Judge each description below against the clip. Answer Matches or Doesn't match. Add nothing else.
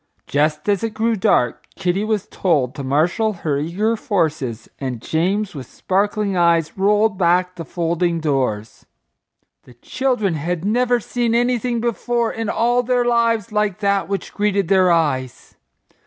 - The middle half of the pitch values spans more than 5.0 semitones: Matches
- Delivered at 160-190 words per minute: Doesn't match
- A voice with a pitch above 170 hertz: Matches